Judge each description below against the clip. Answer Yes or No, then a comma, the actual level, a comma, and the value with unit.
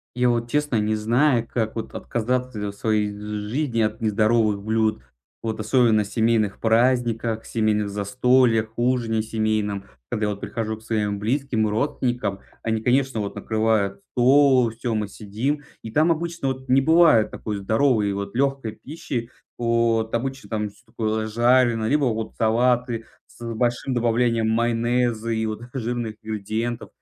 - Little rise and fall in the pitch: Yes, narrow, 2.3 semitones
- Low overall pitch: Yes, low, 115 Hz